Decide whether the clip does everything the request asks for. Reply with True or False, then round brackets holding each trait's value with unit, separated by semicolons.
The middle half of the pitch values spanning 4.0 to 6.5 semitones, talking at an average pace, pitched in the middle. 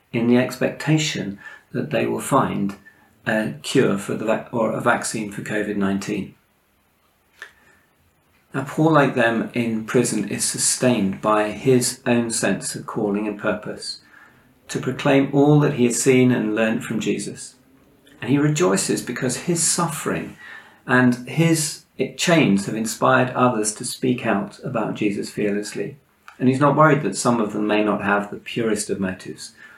False (4.3 semitones; 155 wpm; 125 Hz)